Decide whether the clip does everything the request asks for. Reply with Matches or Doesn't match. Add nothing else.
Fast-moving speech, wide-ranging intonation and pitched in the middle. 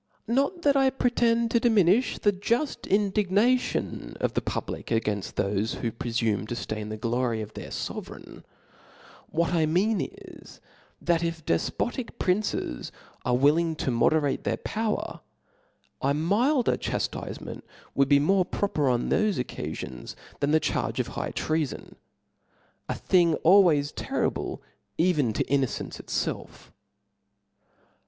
Doesn't match